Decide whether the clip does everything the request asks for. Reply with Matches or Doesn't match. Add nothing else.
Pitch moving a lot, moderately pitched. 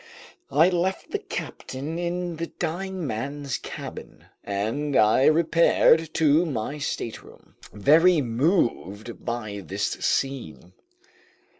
Matches